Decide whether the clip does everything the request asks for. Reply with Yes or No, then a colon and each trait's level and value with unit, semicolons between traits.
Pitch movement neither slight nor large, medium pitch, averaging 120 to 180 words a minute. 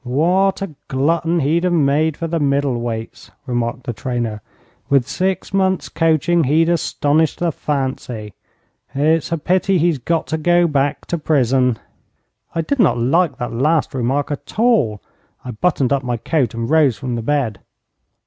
Yes: average, 5.0 semitones; medium, 145 Hz; average, 165 wpm